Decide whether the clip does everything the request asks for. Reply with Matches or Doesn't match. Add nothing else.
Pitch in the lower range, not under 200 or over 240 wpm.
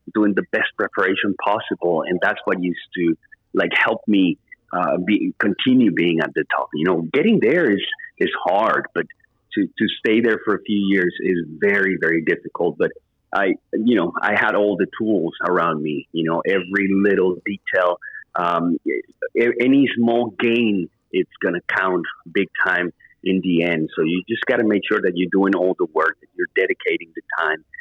Doesn't match